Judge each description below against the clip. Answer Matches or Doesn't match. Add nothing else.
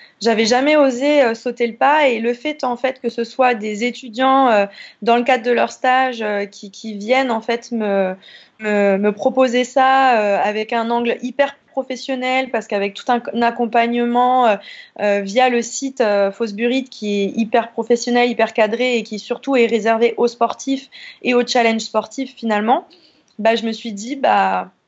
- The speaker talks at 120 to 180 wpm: Doesn't match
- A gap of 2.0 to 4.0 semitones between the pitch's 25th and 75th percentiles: Matches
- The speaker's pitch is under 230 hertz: Doesn't match